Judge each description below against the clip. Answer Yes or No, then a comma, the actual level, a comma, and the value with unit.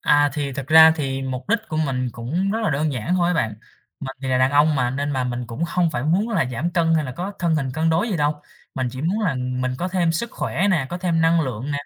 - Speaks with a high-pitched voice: No, medium, 150 Hz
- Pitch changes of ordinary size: Yes, average, 4.7 semitones